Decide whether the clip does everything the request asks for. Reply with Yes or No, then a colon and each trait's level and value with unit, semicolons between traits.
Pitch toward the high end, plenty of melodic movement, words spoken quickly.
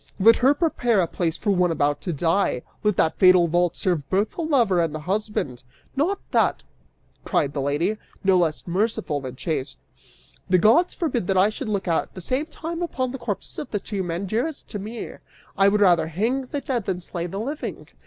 Yes: high, 195 Hz; wide, 5.8 semitones; fast, 210 wpm